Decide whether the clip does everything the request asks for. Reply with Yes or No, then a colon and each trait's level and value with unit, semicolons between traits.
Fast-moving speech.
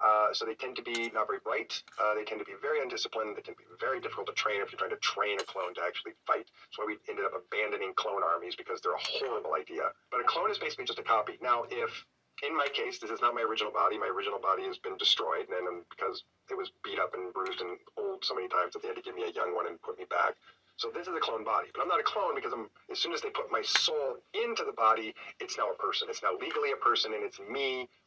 Yes: fast, 285 wpm